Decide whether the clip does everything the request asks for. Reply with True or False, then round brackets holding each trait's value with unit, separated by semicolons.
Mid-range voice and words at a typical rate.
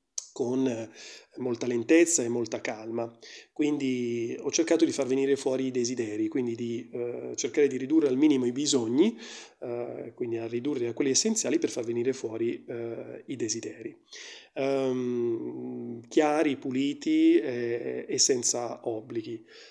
False (130 Hz; 140 wpm)